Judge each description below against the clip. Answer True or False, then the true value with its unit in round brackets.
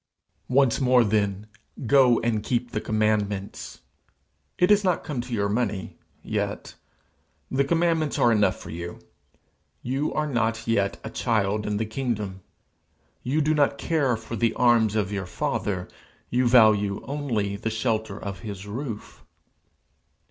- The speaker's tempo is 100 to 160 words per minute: True (145 wpm)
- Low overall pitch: True (115 Hz)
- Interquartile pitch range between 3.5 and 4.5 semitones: True (4.0 semitones)